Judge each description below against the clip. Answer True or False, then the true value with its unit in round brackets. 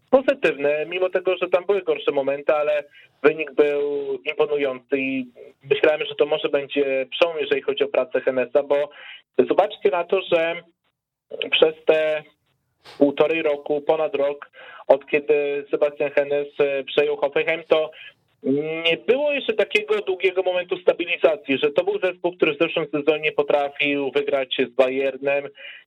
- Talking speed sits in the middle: True (140 wpm)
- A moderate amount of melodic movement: True (4.8 semitones)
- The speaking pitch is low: False (150 Hz)